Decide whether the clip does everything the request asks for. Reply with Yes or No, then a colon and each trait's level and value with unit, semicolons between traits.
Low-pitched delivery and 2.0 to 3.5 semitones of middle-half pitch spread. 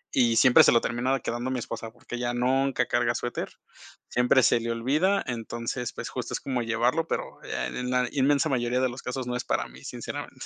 No: low, 125 Hz; narrow, 1.6 semitones